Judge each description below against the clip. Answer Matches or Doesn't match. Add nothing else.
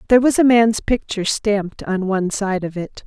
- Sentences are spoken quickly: Matches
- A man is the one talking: Doesn't match